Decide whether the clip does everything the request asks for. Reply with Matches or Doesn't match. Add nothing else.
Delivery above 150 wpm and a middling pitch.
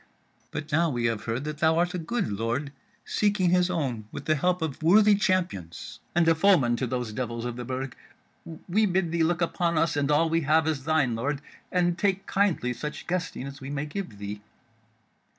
Matches